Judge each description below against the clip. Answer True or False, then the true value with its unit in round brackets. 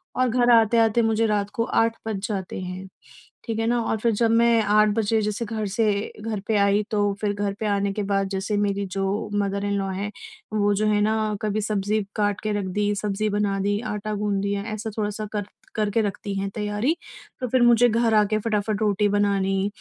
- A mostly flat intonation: True (1.7 semitones)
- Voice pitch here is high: True (210 Hz)